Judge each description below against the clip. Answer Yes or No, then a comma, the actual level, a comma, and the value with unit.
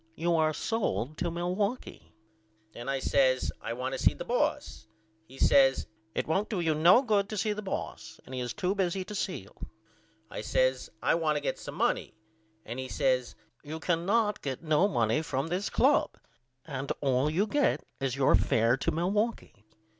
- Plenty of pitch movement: Yes, wide, 7.0 semitones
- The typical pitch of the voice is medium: Yes, medium, 160 Hz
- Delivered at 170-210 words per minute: Yes, average, 185 wpm